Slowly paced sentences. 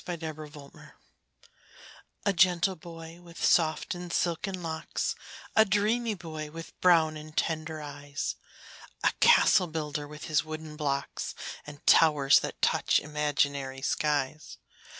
Yes: slow, 130 wpm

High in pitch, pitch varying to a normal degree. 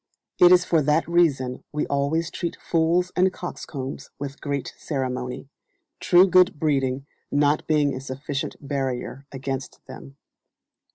No: medium, 145 Hz; average, 3.7 semitones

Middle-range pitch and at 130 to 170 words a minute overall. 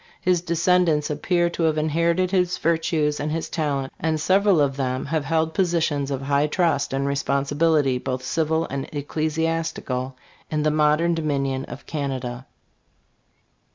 Yes: medium, 155 Hz; average, 150 wpm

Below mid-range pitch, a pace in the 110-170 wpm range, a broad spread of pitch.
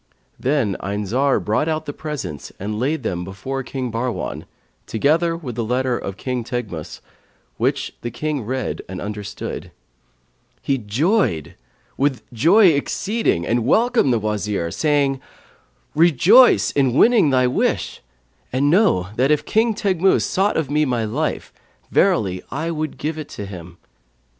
Yes: low, 130 Hz; average, 150 wpm; wide, 6.4 semitones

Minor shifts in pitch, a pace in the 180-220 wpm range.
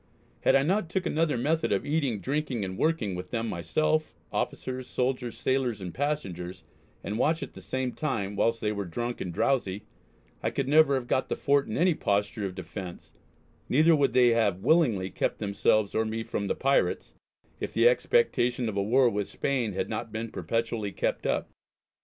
No: wide, 5.6 semitones; average, 190 wpm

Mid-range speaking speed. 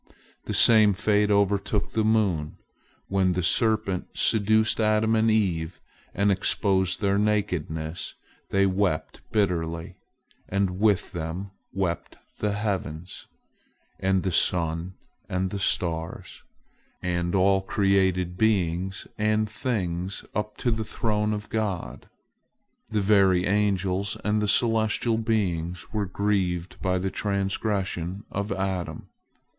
No: slow, 120 wpm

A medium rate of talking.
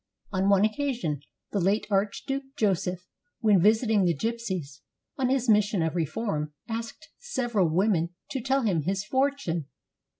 Yes: average, 145 wpm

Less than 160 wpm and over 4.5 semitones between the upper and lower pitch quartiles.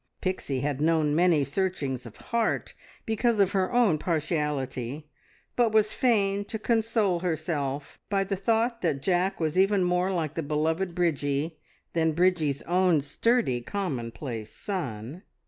Yes: average, 140 wpm; average, 5.1 semitones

